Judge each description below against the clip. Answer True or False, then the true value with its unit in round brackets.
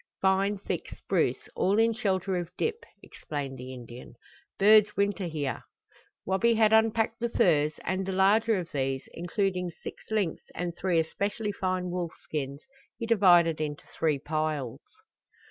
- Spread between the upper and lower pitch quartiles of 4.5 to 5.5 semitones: True (5.0 semitones)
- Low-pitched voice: False (185 Hz)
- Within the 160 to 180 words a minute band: False (145 wpm)